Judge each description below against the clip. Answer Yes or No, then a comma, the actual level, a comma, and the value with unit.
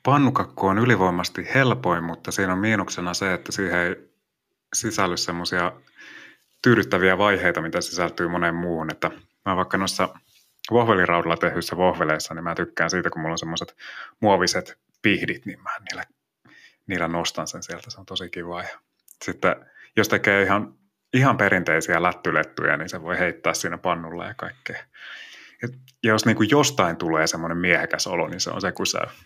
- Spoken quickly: Yes, fast, 160 wpm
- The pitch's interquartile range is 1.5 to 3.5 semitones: Yes, average, 2.9 semitones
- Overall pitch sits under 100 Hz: Yes, very low, 90 Hz